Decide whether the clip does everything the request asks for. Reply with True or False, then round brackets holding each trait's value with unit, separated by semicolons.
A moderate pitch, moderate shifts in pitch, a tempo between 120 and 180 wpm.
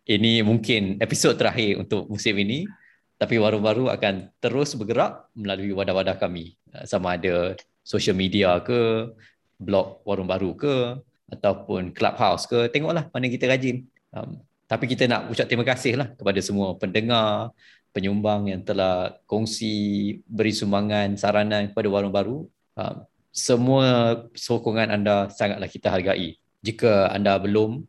False (110 Hz; 3.3 semitones; 135 wpm)